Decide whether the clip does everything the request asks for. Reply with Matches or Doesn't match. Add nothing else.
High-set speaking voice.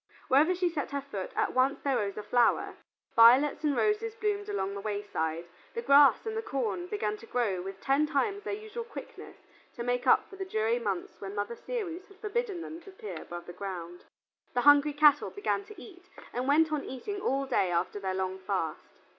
Matches